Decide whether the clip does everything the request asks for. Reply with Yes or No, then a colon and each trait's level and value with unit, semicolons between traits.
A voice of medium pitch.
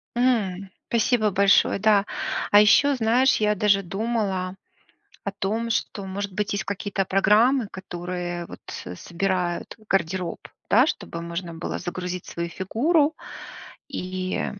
No: high, 195 Hz